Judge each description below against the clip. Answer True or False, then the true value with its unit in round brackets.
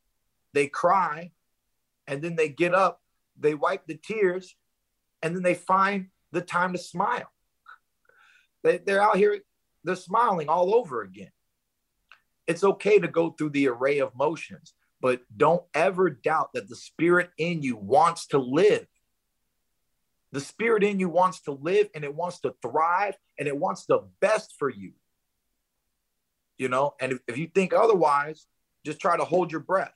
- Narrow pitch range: False (4.3 semitones)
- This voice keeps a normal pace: True (165 wpm)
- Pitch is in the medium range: True (175 Hz)